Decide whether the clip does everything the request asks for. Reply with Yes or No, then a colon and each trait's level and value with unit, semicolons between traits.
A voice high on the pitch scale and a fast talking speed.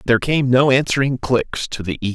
No: low, 125 Hz; fast, 250 wpm